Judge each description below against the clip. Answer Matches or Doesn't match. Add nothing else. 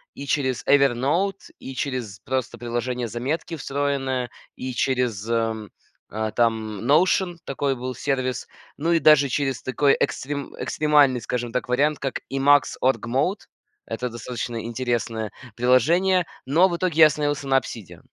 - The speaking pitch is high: Doesn't match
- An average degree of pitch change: Matches